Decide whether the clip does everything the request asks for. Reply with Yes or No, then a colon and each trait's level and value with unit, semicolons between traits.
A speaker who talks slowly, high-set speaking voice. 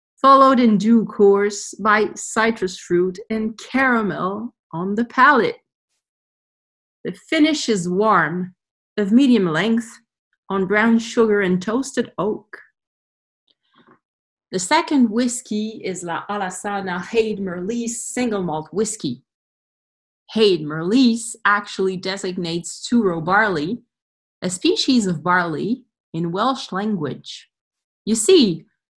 Yes: slow, 105 wpm; high, 210 Hz